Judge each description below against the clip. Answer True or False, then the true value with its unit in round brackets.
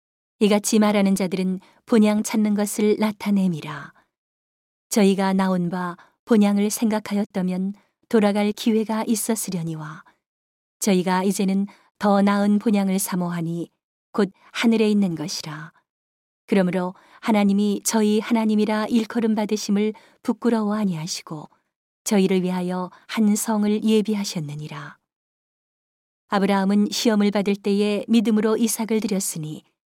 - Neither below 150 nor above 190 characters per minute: False (285 characters per minute)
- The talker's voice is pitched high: True (205 Hz)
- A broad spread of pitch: False (2.3 semitones)